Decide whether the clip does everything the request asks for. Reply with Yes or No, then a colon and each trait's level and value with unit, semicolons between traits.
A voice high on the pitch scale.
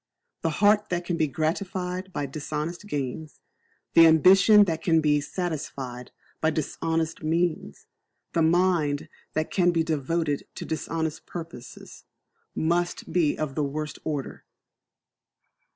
No: medium, 160 Hz